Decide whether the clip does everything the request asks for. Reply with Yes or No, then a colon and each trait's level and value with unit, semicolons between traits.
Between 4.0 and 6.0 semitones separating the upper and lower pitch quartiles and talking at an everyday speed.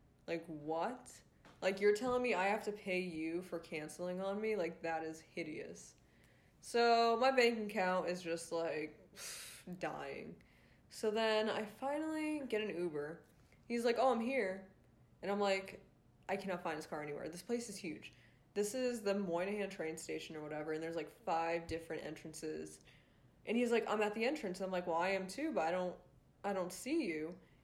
Yes: average, 4.8 semitones; average, 190 wpm